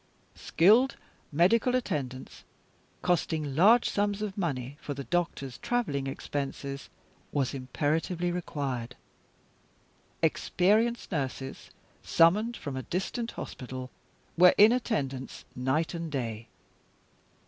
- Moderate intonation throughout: No, wide, 7.0 semitones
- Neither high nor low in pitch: Yes, medium, 155 Hz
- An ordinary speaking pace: No, slow, 100 wpm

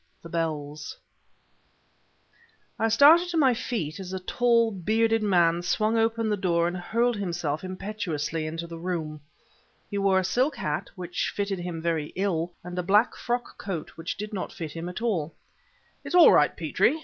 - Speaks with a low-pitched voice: No, medium, 185 Hz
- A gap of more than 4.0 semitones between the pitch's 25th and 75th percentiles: Yes, average, 5.0 semitones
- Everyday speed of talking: Yes, average, 175 wpm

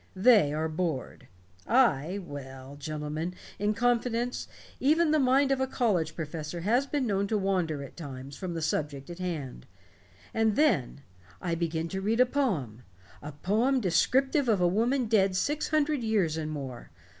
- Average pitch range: No, wide, 7.9 semitones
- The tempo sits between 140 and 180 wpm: Yes, average, 165 wpm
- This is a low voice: No, medium, 185 Hz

